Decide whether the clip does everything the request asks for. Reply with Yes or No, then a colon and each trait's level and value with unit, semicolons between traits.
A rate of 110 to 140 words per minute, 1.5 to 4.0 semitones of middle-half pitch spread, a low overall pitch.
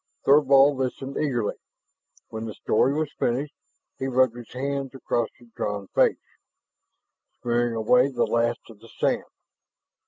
Yes: slow, 135 wpm; average, 2.8 semitones; low, 125 Hz